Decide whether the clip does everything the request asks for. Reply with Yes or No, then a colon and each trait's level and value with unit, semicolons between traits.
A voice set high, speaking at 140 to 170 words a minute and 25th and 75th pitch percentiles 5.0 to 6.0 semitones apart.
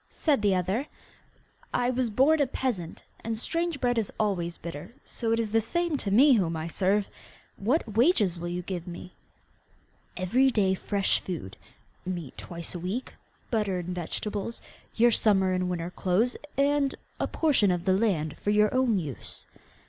Yes: high, 205 Hz; average, 165 wpm; average, 5.3 semitones